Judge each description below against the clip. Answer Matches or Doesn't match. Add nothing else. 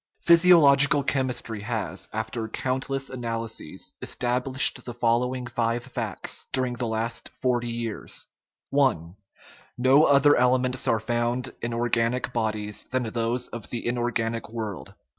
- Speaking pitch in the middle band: Doesn't match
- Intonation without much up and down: Matches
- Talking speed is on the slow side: Matches